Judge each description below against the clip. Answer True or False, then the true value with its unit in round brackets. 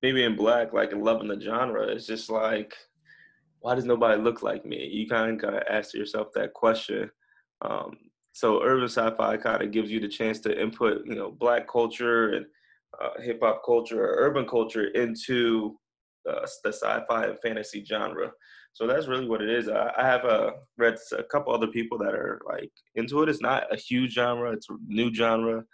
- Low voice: True (115 Hz)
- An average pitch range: False (1.8 semitones)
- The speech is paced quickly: True (210 wpm)